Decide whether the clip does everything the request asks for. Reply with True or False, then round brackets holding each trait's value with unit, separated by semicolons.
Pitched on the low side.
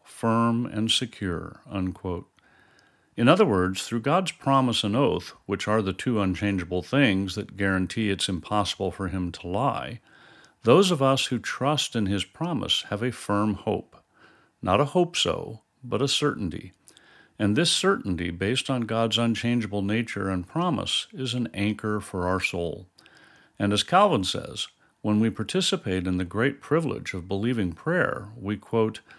True (105 Hz)